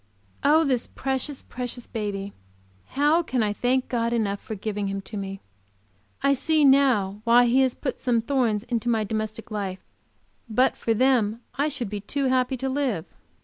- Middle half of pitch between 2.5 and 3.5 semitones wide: No, average, 4.0 semitones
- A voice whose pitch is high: Yes, high, 240 Hz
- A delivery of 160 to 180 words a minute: Yes, average, 175 wpm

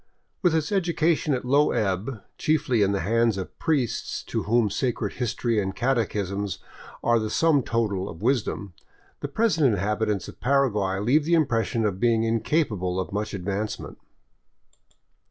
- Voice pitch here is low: Yes, low, 115 Hz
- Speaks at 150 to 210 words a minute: Yes, average, 155 wpm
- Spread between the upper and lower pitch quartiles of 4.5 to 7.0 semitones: Yes, average, 5.3 semitones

